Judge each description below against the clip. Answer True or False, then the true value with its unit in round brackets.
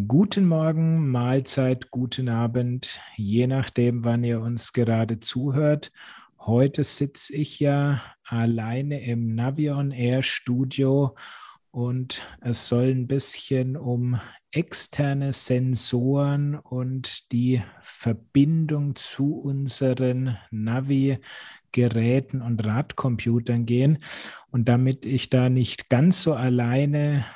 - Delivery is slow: True (105 wpm)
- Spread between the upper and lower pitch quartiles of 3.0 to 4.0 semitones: False (2.5 semitones)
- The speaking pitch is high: False (130 Hz)